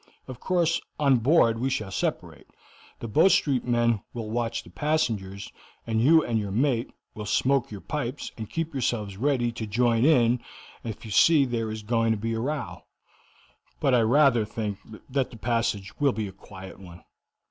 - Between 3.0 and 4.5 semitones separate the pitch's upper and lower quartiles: Yes, average, 3.8 semitones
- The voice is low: Yes, low, 115 Hz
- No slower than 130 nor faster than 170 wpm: No, average, 180 wpm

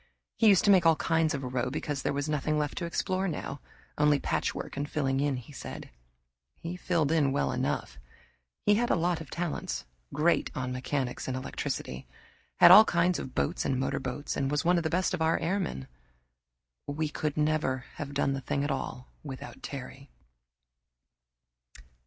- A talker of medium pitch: Yes, medium, 145 Hz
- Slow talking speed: No, average, 180 wpm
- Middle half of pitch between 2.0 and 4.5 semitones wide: Yes, average, 3.7 semitones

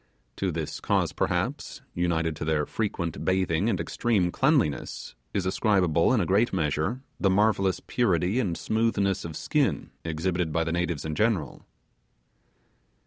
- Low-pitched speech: Yes, very low, 90 Hz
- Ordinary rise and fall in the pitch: Yes, average, 4.4 semitones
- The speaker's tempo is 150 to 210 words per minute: No, average, 140 wpm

